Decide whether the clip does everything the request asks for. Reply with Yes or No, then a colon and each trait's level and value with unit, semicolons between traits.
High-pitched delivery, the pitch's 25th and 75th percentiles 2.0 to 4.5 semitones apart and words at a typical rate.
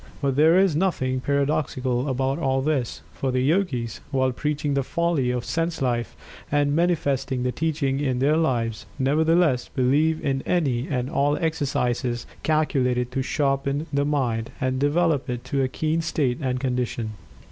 No: low, 135 Hz; average, 3.3 semitones; average, 160 wpm